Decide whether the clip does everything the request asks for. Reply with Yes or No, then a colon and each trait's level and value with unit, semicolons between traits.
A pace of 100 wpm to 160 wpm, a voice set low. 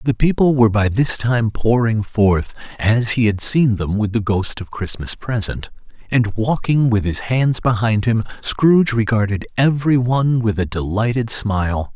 No: average, 170 wpm; low, 115 Hz